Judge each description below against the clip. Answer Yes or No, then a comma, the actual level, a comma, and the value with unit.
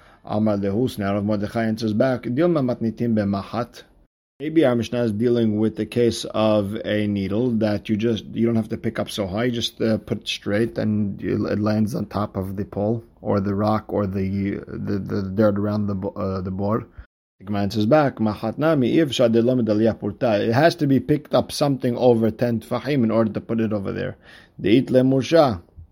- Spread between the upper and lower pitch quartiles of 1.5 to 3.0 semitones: Yes, narrow, 2.6 semitones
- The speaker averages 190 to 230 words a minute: No, average, 165 wpm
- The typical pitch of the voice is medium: No, low, 110 Hz